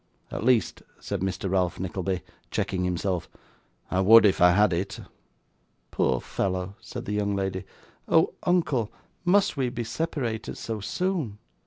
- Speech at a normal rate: Yes, average, 145 wpm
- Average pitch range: Yes, average, 4.2 semitones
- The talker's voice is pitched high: No, low, 100 Hz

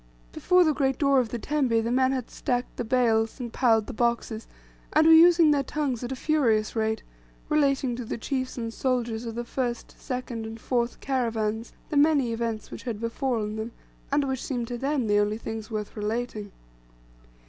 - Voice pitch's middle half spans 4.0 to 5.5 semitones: No, average, 3.2 semitones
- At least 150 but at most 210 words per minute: Yes, average, 190 wpm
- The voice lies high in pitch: Yes, high, 240 Hz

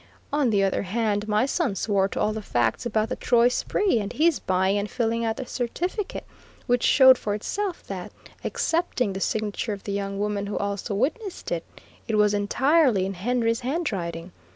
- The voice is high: Yes, high, 215 Hz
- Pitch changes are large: No, average, 4.1 semitones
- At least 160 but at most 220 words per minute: Yes, average, 185 wpm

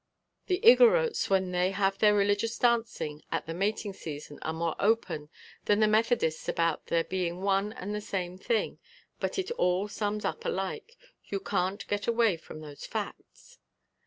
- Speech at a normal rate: Yes, average, 165 wpm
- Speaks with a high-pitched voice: Yes, high, 200 Hz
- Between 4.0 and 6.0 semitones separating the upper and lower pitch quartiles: No, average, 3.6 semitones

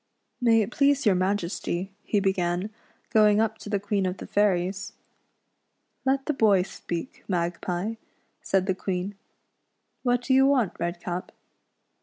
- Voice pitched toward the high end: Yes, high, 200 Hz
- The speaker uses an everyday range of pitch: Yes, average, 3.6 semitones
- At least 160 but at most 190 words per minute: No, average, 145 wpm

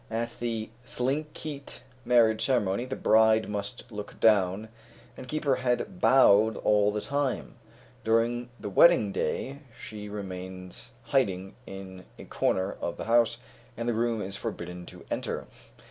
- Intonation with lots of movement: No, average, 3.5 semitones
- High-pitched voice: No, low, 110 Hz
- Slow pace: No, average, 145 wpm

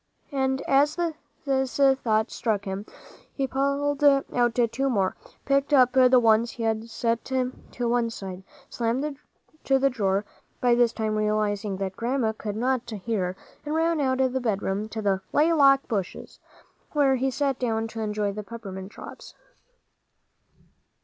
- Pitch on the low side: No, high, 235 Hz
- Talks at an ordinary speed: Yes, average, 150 wpm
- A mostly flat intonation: No, average, 4.0 semitones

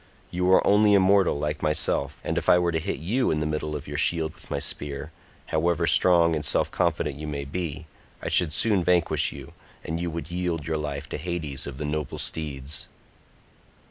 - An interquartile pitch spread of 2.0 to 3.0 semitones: Yes, average, 2.7 semitones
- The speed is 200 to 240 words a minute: Yes, fast, 205 wpm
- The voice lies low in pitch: Yes, very low, 80 Hz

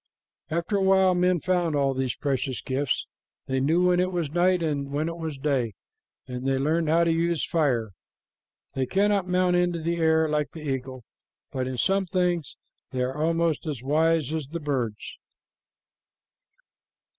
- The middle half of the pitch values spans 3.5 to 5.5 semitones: Yes, average, 4.4 semitones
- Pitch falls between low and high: Yes, medium, 160 Hz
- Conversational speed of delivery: Yes, average, 170 wpm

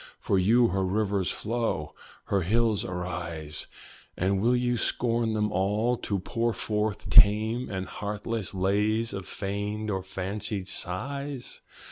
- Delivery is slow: Yes, slow, 130 wpm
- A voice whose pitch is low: Yes, low, 105 Hz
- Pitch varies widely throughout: No, average, 3.2 semitones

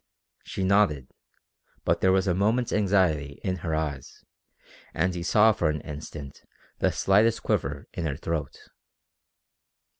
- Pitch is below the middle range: Yes, very low, 85 Hz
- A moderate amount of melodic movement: Yes, average, 4.7 semitones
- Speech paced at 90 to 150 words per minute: Yes, average, 140 wpm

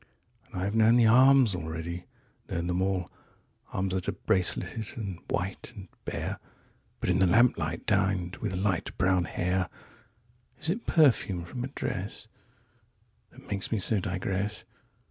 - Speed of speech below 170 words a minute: Yes, average, 140 wpm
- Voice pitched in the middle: No, very low, 95 Hz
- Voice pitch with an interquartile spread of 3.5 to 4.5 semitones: Yes, average, 3.9 semitones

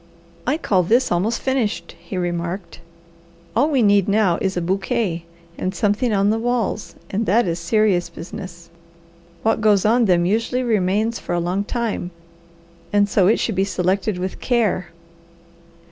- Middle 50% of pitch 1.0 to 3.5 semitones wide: No, average, 3.9 semitones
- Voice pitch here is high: Yes, high, 200 Hz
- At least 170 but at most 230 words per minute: No, average, 160 wpm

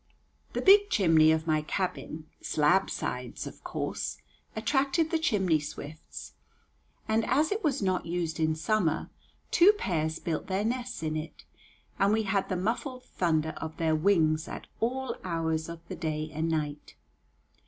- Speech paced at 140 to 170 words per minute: Yes, average, 155 wpm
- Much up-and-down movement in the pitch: Yes, wide, 6.0 semitones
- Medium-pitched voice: Yes, medium, 170 Hz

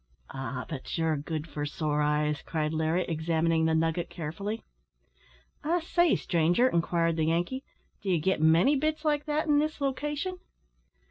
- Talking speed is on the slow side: No, average, 150 wpm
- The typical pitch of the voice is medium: Yes, medium, 165 Hz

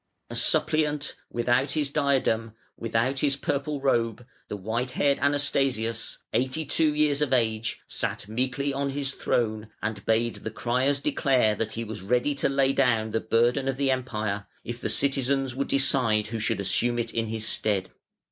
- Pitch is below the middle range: Yes, low, 125 Hz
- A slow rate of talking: No, average, 170 wpm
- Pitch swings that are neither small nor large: Yes, average, 3.7 semitones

